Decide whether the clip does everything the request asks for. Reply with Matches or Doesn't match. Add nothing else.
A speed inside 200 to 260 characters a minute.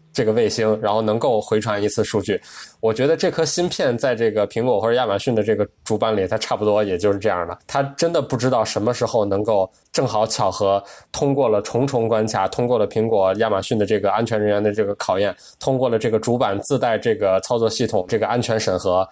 Doesn't match